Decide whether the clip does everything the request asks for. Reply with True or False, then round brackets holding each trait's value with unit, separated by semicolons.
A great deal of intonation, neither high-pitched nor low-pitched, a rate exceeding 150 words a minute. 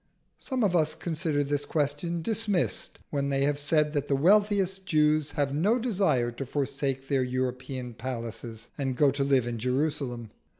False (3.9 semitones; 145 Hz; 165 wpm)